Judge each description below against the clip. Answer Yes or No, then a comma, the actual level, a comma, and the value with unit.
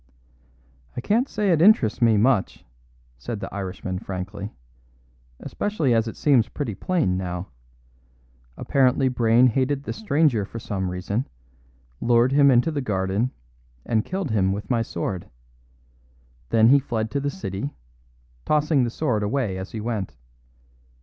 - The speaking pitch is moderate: No, low, 115 Hz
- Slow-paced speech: No, average, 145 wpm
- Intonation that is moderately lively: No, wide, 5.7 semitones